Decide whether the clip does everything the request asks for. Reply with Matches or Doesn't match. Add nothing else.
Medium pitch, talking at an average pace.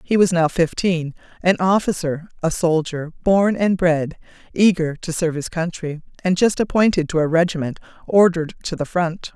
Matches